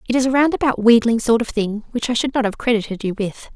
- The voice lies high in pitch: Yes, high, 235 Hz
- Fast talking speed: Yes, fast, 270 wpm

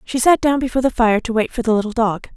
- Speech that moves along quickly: Yes, fast, 305 wpm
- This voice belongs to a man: No, female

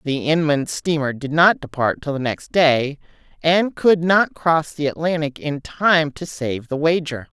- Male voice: No, female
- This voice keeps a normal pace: Yes, average, 180 wpm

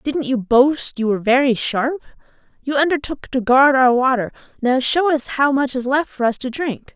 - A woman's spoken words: Yes, female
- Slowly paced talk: No, fast, 205 wpm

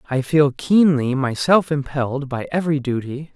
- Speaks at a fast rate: No, average, 145 wpm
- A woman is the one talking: No, male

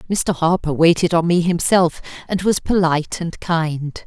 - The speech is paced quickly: No, average, 160 wpm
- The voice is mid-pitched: Yes, medium, 170 Hz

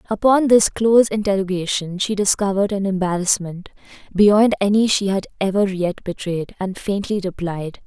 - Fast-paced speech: No, slow, 135 wpm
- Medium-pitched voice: No, high, 195 Hz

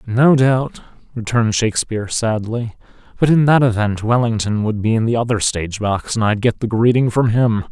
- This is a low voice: Yes, low, 115 Hz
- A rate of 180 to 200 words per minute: Yes, average, 185 wpm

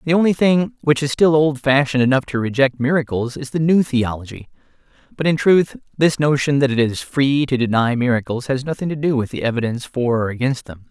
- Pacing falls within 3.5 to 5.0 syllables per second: No, 5.7 syllables/s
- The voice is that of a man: Yes, male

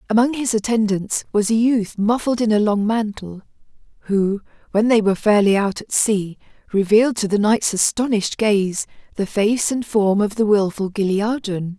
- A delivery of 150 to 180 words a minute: Yes, average, 170 wpm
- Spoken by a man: No, female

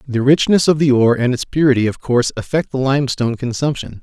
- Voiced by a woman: No, male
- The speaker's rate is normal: No, fast, 210 wpm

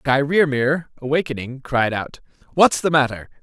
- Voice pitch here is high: No, medium, 140 Hz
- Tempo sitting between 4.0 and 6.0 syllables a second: Yes, 4.4 syllables/s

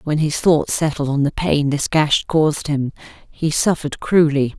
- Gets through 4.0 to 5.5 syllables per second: Yes, 4.6 syllables/s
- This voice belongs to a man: No, female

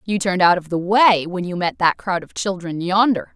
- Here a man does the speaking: No, female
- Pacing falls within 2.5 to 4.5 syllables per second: No, 5.3 syllables/s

